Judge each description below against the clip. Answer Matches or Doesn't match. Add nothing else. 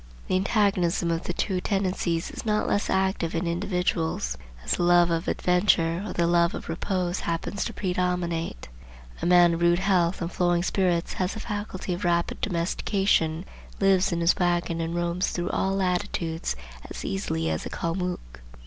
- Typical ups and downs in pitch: Doesn't match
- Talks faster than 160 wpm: Matches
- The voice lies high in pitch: Doesn't match